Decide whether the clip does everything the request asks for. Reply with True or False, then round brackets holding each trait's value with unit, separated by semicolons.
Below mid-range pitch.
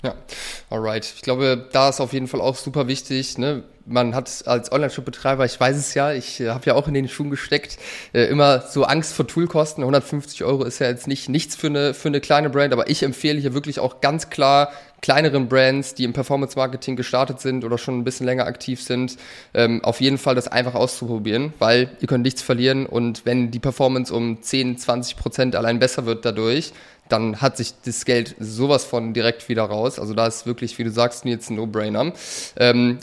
True (130 Hz)